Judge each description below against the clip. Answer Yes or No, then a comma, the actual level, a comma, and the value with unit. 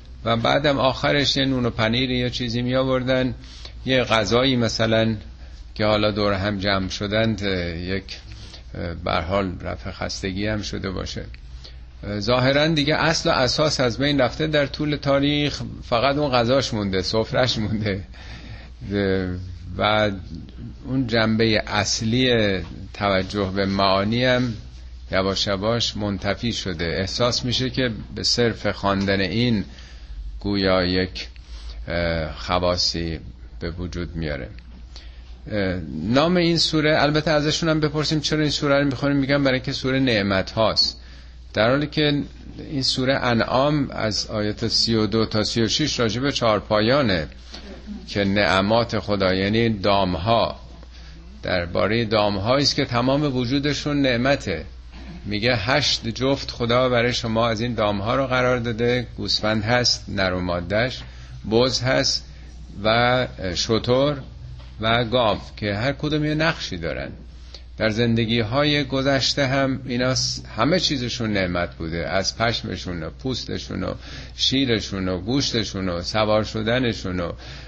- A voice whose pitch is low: Yes, low, 110 Hz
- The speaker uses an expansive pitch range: Yes, wide, 5.7 semitones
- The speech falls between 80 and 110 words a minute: No, average, 125 wpm